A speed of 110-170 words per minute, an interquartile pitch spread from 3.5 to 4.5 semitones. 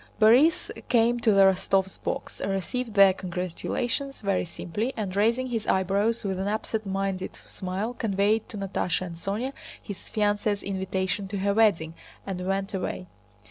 No: average, 150 wpm; average, 2.7 semitones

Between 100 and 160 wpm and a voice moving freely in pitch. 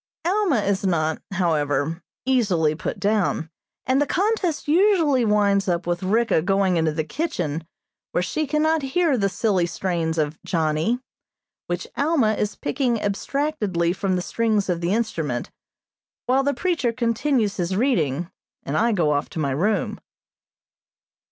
Yes: average, 145 wpm; wide, 7.6 semitones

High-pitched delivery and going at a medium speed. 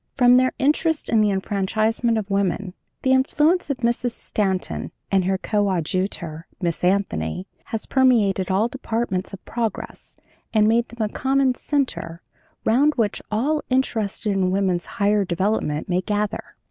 Yes: high, 210 Hz; average, 145 wpm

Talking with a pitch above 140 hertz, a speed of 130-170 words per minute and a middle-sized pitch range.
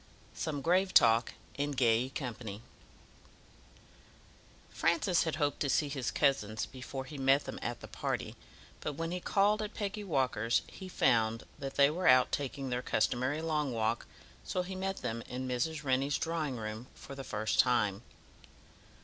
No: low, 135 Hz; average, 160 wpm; average, 4.9 semitones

